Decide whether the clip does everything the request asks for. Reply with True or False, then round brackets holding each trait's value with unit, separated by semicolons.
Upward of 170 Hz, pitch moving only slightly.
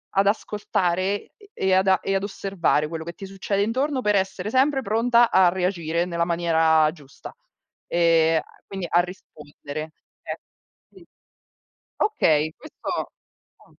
False (185 Hz; 3.7 semitones)